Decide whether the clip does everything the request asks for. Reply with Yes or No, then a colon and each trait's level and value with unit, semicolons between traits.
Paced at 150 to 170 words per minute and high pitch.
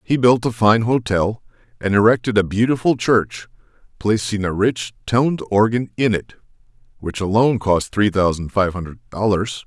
No: average, 155 wpm; low, 110 Hz